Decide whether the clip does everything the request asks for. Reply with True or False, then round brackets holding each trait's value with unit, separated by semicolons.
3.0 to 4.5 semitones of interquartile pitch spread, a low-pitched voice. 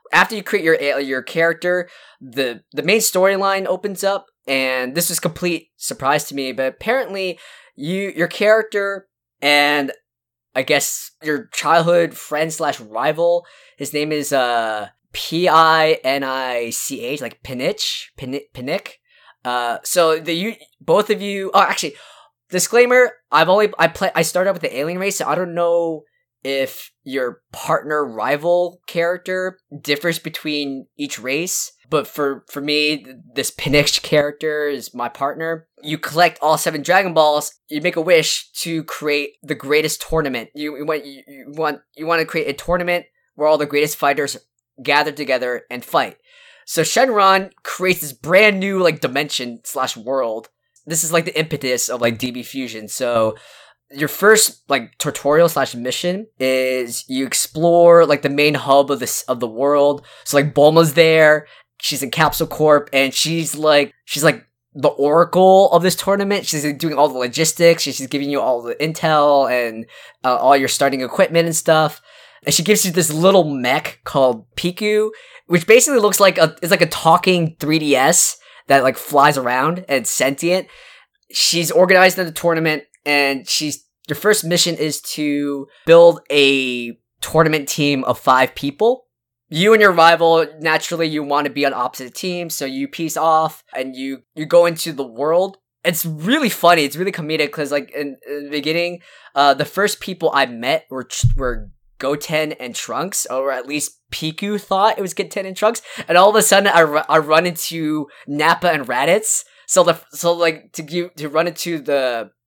False (4.0 semitones; 155 Hz)